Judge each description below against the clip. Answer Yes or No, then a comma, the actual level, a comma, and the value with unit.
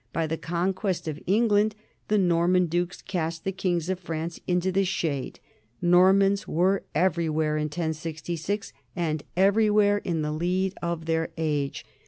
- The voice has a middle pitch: Yes, medium, 175 Hz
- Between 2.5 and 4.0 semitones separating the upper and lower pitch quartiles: Yes, average, 2.9 semitones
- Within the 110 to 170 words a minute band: Yes, average, 145 wpm